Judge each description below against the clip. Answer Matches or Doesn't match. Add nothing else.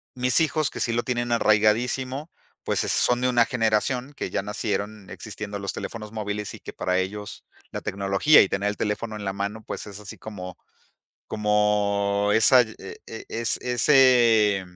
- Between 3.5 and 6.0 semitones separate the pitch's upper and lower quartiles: Doesn't match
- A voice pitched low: Matches